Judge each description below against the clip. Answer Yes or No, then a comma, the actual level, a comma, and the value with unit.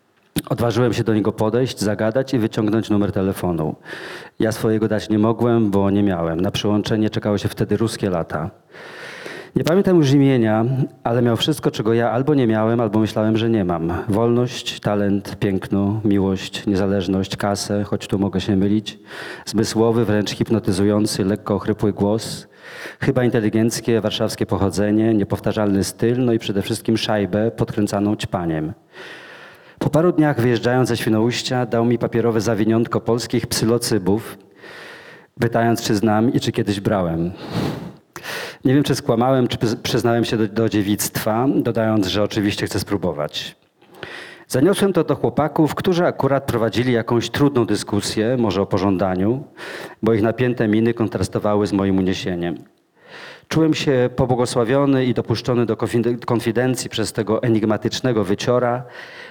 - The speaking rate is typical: Yes, average, 140 wpm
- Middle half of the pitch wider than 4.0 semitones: No, average, 2.9 semitones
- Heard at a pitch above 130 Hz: No, low, 115 Hz